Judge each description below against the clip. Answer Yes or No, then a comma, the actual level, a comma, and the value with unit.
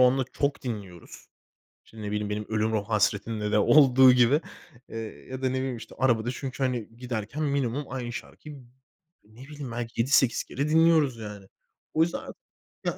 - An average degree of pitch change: Yes, average, 3.6 semitones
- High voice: No, low, 125 Hz